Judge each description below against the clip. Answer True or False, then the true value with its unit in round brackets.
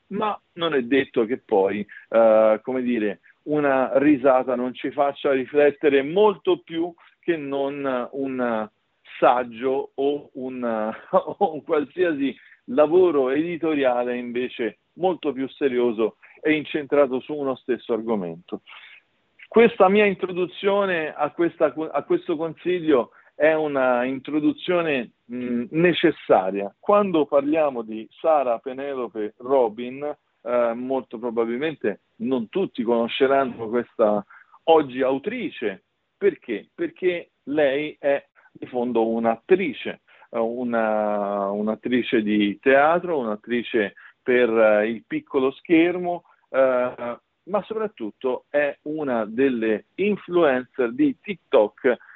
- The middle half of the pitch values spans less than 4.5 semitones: False (5.6 semitones)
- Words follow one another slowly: True (105 wpm)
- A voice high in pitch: False (140 Hz)